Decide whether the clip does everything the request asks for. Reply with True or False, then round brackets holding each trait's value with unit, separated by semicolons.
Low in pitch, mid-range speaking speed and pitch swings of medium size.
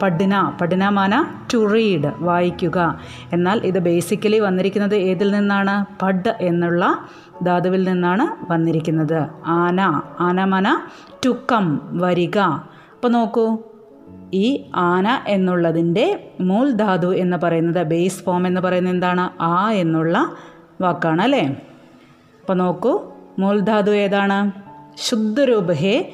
False (185 Hz; 100 wpm; 3.0 semitones)